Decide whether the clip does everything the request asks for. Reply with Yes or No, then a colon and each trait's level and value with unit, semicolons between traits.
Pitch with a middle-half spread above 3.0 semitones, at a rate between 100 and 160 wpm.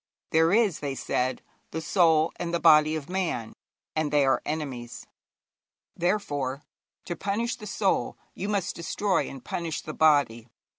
Yes: average, 4.6 semitones; average, 150 wpm